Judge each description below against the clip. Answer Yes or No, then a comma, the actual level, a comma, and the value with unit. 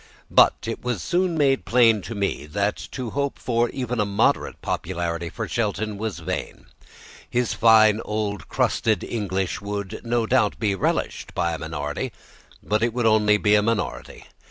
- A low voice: Yes, low, 105 Hz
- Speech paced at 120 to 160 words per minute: No, average, 170 wpm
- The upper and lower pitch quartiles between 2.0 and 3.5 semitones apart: Yes, average, 2.9 semitones